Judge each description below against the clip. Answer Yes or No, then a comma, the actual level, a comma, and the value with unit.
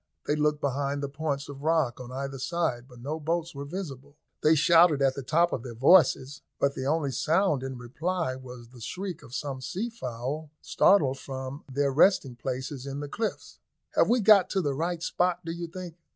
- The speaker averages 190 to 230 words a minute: Yes, average, 200 wpm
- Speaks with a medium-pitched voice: Yes, medium, 145 Hz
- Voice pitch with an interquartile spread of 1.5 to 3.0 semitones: No, average, 4.1 semitones